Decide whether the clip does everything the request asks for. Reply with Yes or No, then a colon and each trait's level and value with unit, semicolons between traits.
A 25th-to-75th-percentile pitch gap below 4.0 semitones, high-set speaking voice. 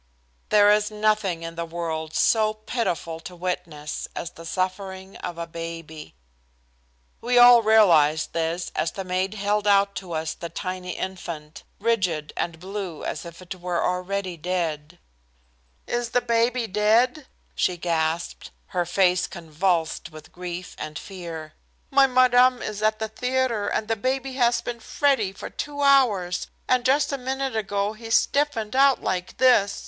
No: average, 5.2 semitones; high, 195 Hz